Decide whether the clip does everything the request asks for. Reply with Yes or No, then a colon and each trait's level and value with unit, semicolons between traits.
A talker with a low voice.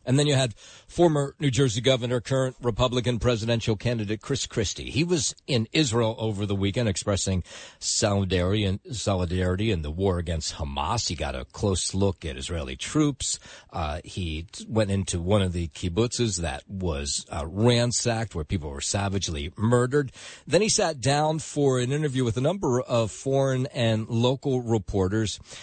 Yes: low, 110 Hz